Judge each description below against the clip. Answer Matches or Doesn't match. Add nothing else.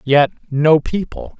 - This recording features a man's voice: Matches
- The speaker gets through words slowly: Matches